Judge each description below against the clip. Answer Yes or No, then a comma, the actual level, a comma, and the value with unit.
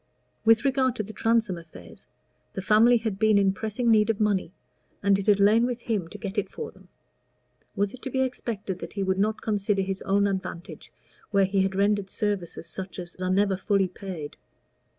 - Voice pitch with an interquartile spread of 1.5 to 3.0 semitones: Yes, narrow, 2.5 semitones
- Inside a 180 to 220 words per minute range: Yes, average, 200 wpm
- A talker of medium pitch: No, high, 200 Hz